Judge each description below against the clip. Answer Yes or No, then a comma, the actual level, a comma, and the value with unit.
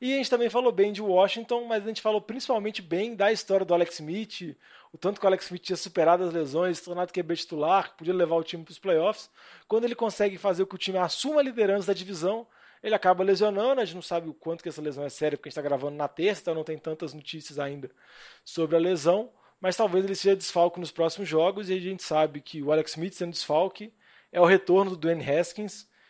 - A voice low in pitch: No, medium, 185 Hz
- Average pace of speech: No, fast, 245 wpm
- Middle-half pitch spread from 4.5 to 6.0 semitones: No, average, 3.8 semitones